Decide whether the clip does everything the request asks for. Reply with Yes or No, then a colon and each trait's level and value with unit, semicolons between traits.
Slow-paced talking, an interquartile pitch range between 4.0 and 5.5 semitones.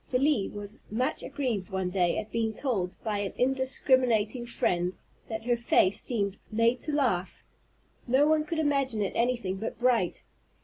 No: average, 160 wpm; average, 4.5 semitones